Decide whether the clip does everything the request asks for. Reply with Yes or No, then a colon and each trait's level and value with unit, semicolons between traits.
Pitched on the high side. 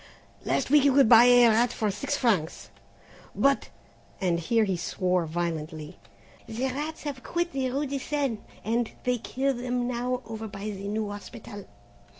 Yes: high, 235 Hz